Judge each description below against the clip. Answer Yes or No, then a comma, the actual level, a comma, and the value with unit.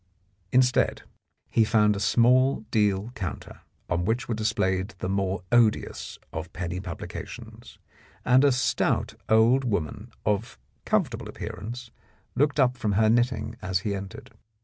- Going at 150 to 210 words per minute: No, slow, 135 wpm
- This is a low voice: Yes, low, 110 Hz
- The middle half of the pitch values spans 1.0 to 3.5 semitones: No, average, 4.2 semitones